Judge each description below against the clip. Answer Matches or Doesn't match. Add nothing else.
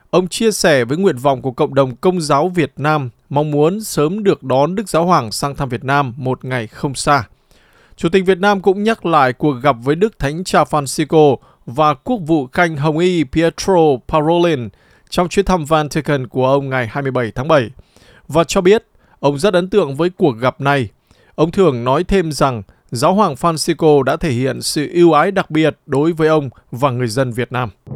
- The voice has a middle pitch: Matches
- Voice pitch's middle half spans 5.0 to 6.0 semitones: Doesn't match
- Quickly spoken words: Doesn't match